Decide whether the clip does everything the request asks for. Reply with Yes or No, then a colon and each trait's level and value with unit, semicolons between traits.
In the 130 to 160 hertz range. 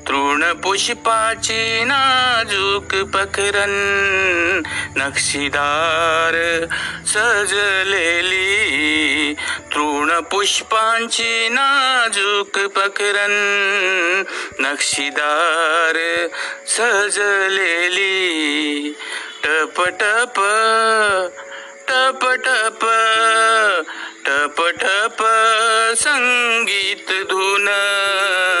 No: high, 200 Hz